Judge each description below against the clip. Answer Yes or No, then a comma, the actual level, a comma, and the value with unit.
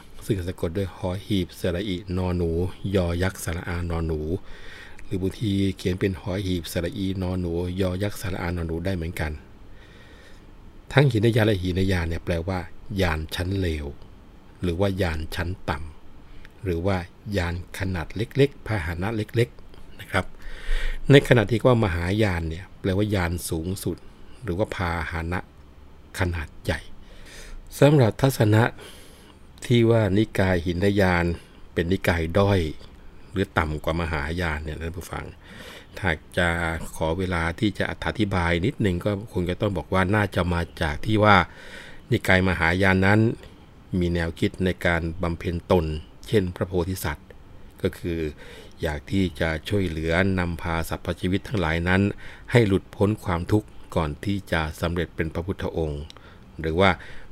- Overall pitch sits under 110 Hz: Yes, very low, 95 Hz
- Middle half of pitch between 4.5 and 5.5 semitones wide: No, average, 2.8 semitones